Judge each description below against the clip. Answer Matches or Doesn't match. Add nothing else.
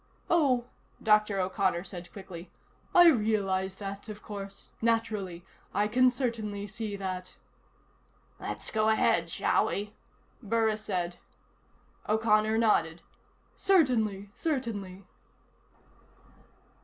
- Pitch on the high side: Matches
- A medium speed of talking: Doesn't match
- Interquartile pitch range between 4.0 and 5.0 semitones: Doesn't match